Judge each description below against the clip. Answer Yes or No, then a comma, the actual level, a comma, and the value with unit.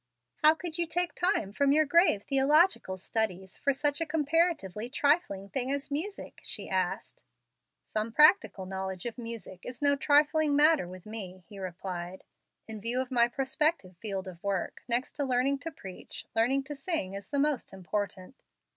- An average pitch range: No, wide, 7.3 semitones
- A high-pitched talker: Yes, very high, 255 Hz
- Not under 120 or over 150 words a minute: No, average, 170 wpm